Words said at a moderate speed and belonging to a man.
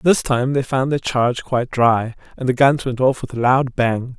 No: fast, 245 wpm; male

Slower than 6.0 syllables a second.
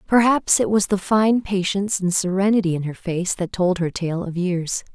Yes: 4.9 syllables/s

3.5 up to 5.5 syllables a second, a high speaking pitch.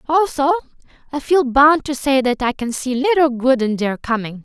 Yes: 4.8 syllables/s; very high, 270 Hz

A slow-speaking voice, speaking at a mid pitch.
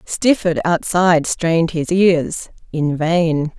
Yes: slow, 100 wpm; medium, 170 Hz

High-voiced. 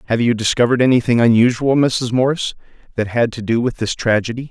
No: low, 120 Hz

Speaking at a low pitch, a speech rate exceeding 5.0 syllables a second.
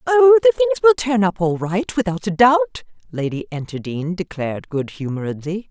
No: high, 190 Hz; 5.3 syllables/s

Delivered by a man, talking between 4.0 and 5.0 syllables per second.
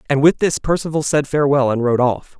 No: male; 6.0 syllables/s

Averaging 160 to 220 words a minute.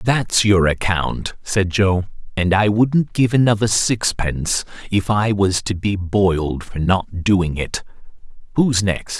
No: average, 150 wpm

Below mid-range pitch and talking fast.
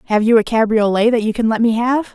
No: high, 225 Hz; fast, 280 wpm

